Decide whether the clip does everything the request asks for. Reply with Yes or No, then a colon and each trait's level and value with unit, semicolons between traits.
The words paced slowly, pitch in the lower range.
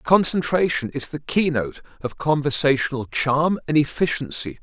No: slow, 115 wpm; medium, 145 Hz